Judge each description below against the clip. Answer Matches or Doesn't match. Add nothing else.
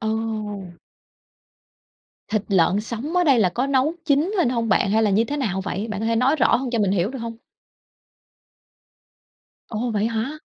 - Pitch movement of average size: Matches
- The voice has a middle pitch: Doesn't match